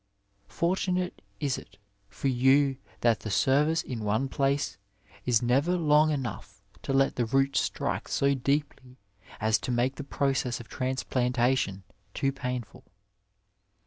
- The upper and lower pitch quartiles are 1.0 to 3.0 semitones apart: Yes, narrow, 2.5 semitones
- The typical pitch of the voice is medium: No, low, 130 Hz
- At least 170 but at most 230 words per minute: No, slow, 135 wpm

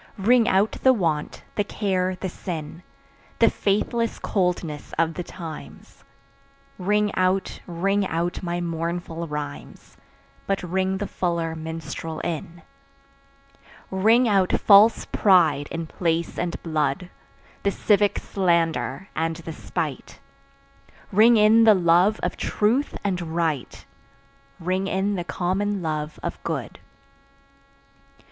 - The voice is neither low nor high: Yes, medium, 180 Hz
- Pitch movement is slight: No, average, 3.4 semitones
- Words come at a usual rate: No, slow, 120 wpm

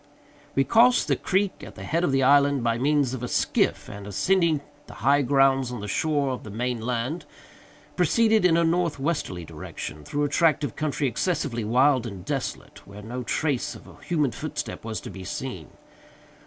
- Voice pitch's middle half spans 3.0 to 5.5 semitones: Yes, average, 4.9 semitones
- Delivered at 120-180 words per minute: No, average, 190 wpm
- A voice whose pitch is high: No, low, 135 Hz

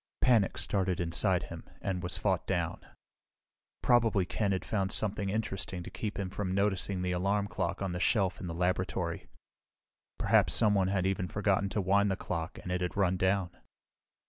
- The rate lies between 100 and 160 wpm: No, average, 175 wpm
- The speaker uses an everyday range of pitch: No, narrow, 1.9 semitones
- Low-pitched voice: Yes, very low, 95 Hz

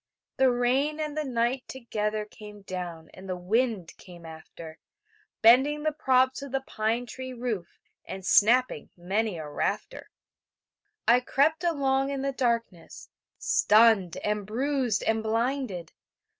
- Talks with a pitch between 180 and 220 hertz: No, high, 235 Hz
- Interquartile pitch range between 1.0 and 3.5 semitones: No, average, 5.1 semitones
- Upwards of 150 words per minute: No, slow, 135 wpm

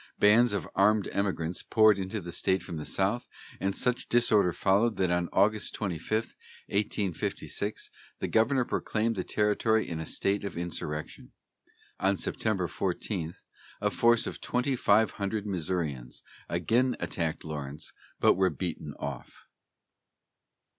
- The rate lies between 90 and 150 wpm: Yes, slow, 135 wpm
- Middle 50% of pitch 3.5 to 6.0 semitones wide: Yes, average, 3.9 semitones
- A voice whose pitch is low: Yes, low, 100 Hz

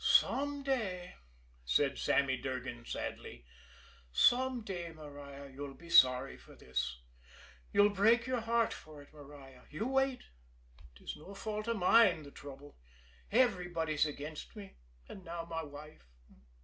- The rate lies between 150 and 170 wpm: No, slow, 135 wpm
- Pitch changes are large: Yes, wide, 7.4 semitones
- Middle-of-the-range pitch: Yes, medium, 160 Hz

